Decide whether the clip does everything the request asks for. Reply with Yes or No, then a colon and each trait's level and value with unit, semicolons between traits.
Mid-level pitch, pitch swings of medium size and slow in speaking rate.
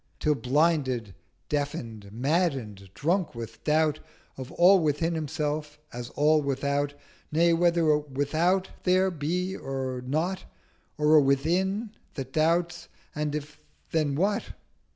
Yes: medium, 150 Hz; average, 3.6 semitones; slow, 125 wpm